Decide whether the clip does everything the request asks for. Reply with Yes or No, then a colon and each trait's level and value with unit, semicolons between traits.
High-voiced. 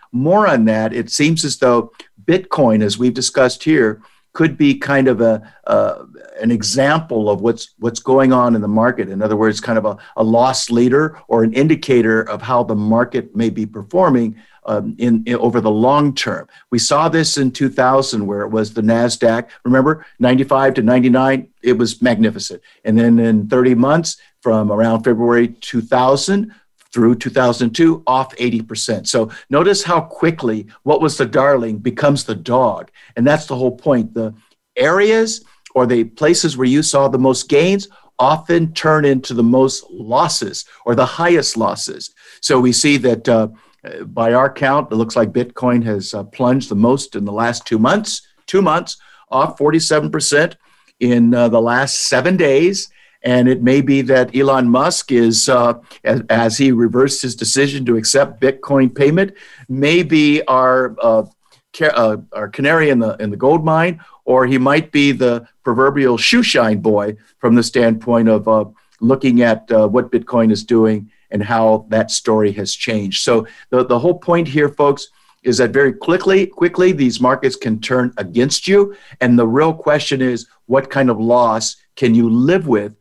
No: low, 125 Hz